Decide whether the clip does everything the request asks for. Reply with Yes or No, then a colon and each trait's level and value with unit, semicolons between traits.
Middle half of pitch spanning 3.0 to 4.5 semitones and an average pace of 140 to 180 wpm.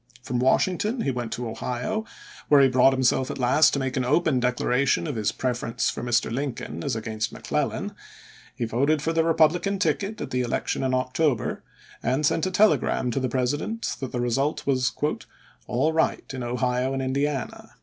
No: average, 3.5 semitones; average, 190 wpm